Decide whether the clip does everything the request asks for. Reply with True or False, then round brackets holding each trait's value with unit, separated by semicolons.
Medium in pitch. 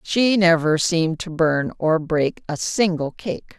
True (170 Hz)